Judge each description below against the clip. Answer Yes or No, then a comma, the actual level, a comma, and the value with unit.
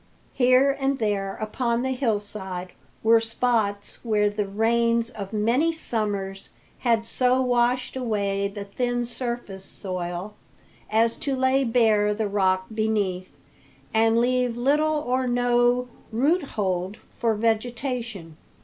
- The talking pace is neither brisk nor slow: No, slow, 120 wpm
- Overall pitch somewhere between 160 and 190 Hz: No, high, 230 Hz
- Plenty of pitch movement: No, average, 3.4 semitones